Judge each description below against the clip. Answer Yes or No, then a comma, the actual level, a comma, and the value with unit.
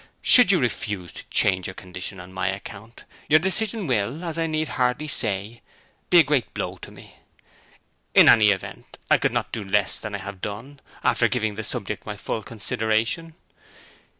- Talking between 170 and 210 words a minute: Yes, average, 180 wpm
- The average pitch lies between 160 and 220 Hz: No, low, 110 Hz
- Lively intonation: Yes, wide, 7.1 semitones